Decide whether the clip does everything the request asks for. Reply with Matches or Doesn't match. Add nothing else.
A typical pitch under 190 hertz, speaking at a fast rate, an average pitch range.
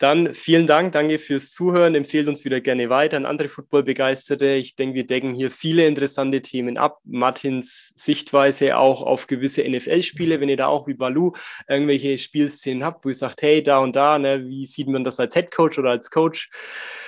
Doesn't match